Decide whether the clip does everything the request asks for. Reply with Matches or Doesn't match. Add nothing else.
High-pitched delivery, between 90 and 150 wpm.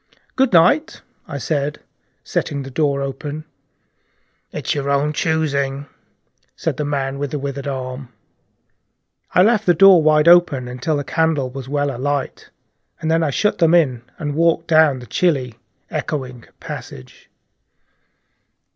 Doesn't match